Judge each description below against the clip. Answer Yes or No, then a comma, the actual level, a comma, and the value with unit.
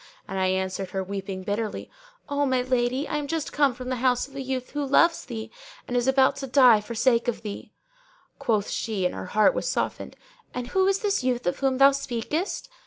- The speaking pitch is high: Yes, very high, 250 Hz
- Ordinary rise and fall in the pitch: Yes, average, 4.3 semitones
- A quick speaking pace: Yes, fast, 225 wpm